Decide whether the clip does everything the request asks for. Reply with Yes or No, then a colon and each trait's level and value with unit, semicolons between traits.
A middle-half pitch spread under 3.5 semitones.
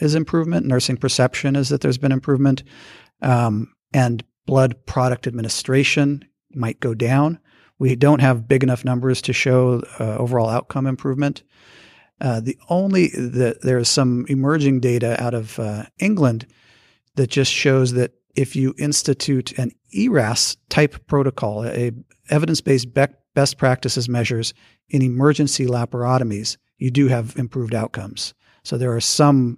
Yes: narrow, 2.4 semitones